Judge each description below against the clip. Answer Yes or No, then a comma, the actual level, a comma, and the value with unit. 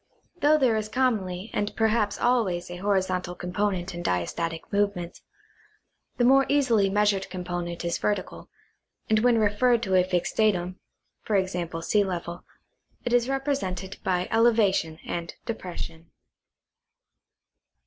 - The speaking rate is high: No, slow, 135 wpm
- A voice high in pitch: Yes, high, 195 Hz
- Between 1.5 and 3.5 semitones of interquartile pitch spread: No, average, 4.1 semitones